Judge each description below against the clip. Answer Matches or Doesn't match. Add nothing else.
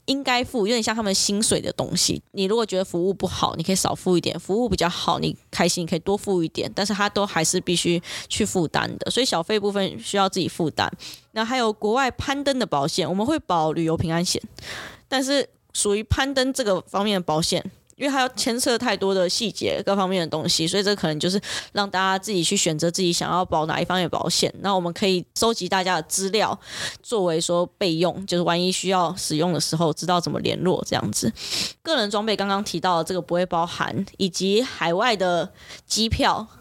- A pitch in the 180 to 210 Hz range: Matches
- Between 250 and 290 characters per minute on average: Doesn't match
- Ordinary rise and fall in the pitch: Matches